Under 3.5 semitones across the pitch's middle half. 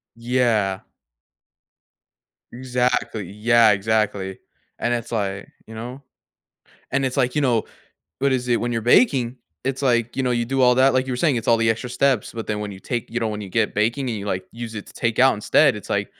Yes: average, 2.7 semitones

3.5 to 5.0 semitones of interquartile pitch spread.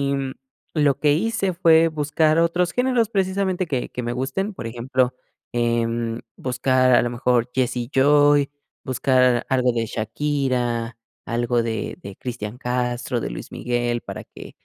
Yes: average, 3.8 semitones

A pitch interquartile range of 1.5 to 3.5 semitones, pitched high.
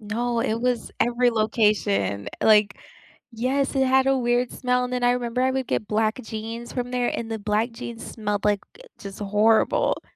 Yes: narrow, 2.6 semitones; high, 230 Hz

